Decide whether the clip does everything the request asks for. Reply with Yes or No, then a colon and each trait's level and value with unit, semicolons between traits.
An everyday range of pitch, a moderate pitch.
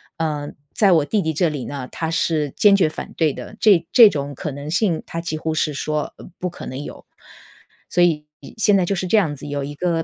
Yes: average, 3.5 semitones; medium, 160 Hz